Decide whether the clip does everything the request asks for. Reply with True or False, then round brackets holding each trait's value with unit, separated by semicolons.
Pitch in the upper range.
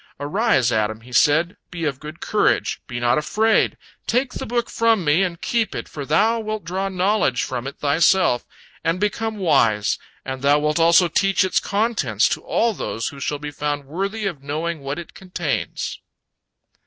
False (165 Hz)